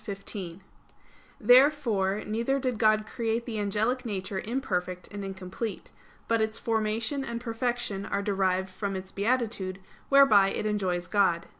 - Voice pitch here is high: Yes, high, 215 Hz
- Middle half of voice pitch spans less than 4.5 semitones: Yes, average, 3.4 semitones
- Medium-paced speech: No, slow, 130 wpm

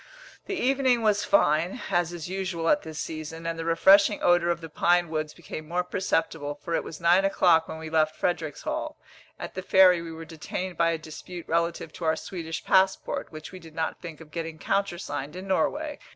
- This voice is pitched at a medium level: Yes, medium, 170 Hz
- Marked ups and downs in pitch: No, average, 2.7 semitones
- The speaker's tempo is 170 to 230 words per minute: Yes, average, 200 wpm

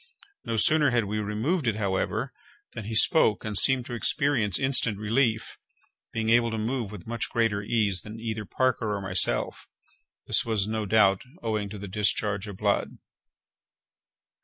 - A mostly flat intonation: Yes, narrow, 2.3 semitones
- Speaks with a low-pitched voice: Yes, low, 110 Hz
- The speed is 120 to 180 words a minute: Yes, average, 155 wpm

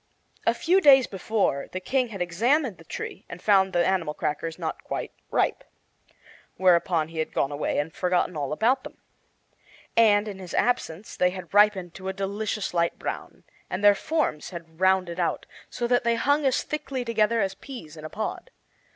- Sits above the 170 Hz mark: Yes, high, 190 Hz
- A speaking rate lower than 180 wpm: No, average, 185 wpm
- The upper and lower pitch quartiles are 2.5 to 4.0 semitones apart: No, average, 5.3 semitones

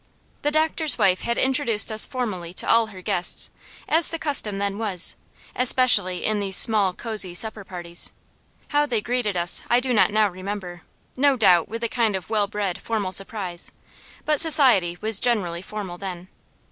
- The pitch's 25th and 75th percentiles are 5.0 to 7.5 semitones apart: No, average, 4.6 semitones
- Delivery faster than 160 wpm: Yes, average, 170 wpm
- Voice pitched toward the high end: Yes, high, 210 Hz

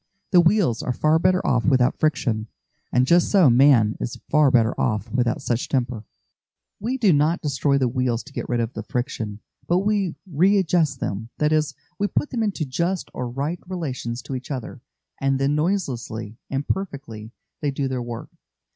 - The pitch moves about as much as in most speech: No, wide, 5.9 semitones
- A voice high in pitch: No, low, 135 Hz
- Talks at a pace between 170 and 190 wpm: Yes, average, 180 wpm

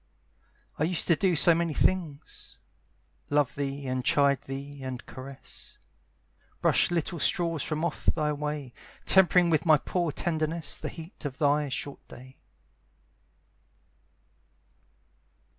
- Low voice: No, medium, 150 Hz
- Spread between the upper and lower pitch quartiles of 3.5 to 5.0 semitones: No, average, 3.1 semitones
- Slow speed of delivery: Yes, slow, 125 wpm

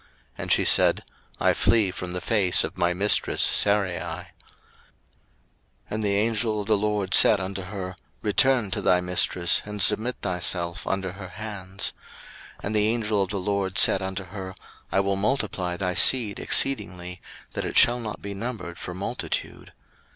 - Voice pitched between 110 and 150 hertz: No, low, 100 Hz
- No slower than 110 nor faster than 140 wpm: No, average, 165 wpm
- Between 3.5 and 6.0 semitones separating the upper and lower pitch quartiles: No, narrow, 2.5 semitones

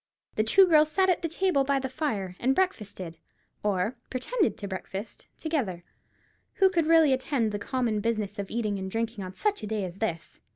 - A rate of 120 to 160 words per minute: No, average, 200 wpm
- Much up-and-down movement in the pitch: Yes, wide, 7.4 semitones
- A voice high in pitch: Yes, high, 230 Hz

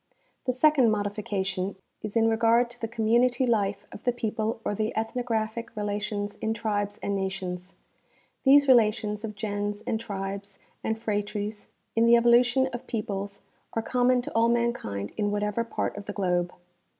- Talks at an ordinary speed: Yes, average, 160 wpm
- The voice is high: Yes, high, 215 Hz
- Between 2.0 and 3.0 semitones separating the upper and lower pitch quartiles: Yes, narrow, 2.4 semitones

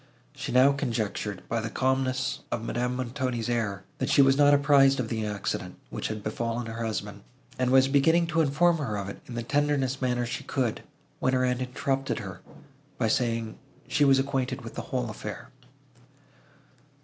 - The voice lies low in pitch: Yes, low, 125 Hz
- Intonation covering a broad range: No, average, 3.0 semitones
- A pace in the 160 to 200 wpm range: Yes, average, 180 wpm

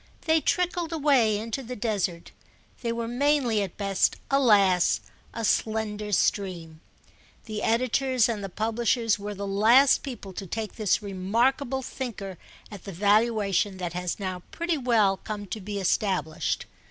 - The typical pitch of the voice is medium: No, high, 215 Hz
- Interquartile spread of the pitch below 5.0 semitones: Yes, average, 3.7 semitones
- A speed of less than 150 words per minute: Yes, average, 140 wpm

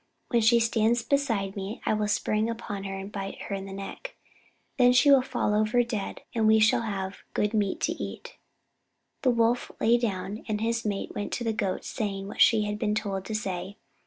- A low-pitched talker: No, high, 215 Hz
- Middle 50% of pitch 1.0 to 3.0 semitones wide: Yes, average, 2.7 semitones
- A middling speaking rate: No, fast, 215 wpm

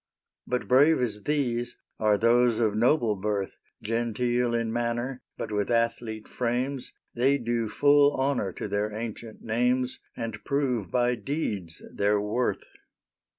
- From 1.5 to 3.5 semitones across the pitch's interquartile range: Yes, narrow, 2.6 semitones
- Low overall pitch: Yes, low, 120 Hz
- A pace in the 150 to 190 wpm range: No, slow, 135 wpm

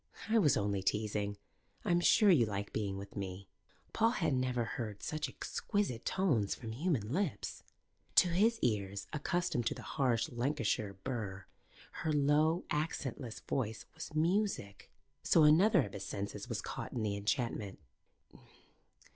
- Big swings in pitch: Yes, wide, 7.5 semitones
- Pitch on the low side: Yes, low, 125 Hz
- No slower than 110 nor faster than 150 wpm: Yes, average, 145 wpm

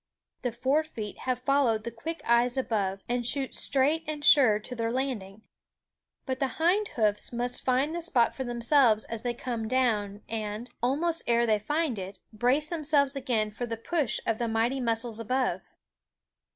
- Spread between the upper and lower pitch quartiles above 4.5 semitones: No, average, 3.5 semitones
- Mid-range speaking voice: No, high, 245 Hz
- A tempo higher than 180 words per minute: No, average, 175 wpm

